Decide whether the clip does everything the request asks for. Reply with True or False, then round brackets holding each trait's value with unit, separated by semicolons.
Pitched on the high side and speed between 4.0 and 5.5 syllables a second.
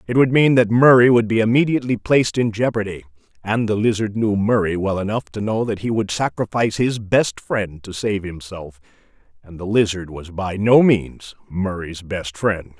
False (105 Hz; 5.0 syllables/s)